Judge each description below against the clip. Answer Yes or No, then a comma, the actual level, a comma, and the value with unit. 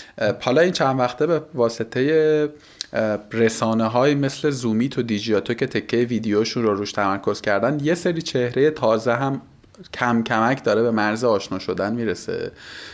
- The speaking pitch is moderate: No, low, 120 Hz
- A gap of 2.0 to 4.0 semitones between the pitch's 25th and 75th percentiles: No, average, 4.4 semitones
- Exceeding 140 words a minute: Yes, average, 150 wpm